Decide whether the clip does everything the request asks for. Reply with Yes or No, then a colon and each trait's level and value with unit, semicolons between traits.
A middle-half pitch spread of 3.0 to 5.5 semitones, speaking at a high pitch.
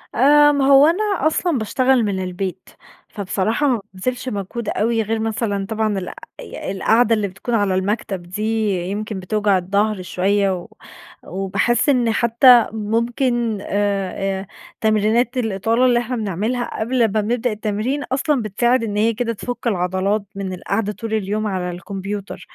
Yes: average, 3.5 semitones; high, 215 Hz